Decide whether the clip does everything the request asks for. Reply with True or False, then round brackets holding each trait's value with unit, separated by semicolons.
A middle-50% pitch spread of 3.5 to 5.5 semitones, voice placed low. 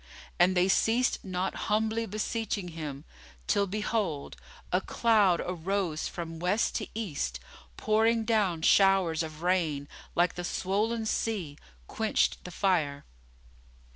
False (4.6 semitones; 185 Hz)